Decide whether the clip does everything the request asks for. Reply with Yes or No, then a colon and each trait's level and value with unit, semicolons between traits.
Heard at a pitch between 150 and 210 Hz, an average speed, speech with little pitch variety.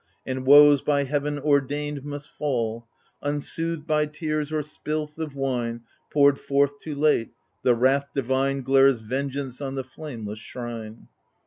No: medium, 140 Hz; average, 145 wpm; narrow, 2.2 semitones